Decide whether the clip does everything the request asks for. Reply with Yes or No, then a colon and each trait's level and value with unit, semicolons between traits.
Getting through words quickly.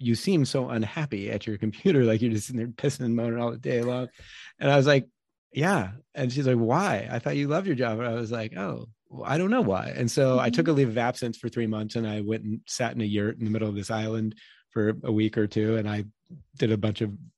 Yes: fast, 275 wpm